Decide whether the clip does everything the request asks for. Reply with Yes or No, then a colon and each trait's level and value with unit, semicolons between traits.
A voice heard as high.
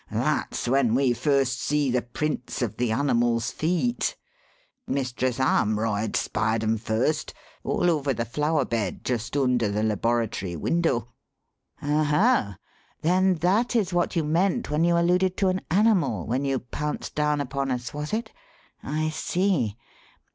No: medium, 140 Hz